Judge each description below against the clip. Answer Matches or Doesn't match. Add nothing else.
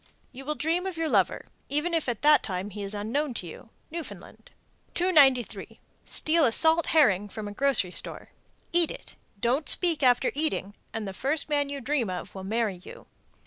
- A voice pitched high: Matches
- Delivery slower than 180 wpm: Doesn't match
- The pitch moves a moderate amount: Doesn't match